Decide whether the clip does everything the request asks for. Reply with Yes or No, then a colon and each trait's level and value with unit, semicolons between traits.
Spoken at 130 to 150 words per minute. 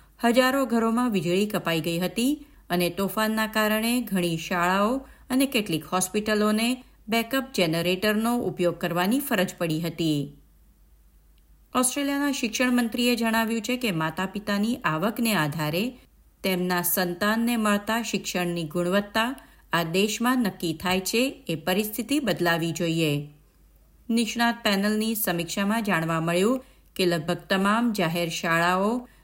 No: average, 115 wpm